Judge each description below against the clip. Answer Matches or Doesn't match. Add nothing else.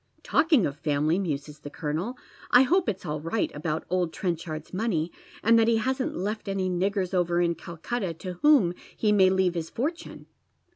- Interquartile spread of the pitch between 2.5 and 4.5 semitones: Doesn't match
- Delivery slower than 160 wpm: Doesn't match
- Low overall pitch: Doesn't match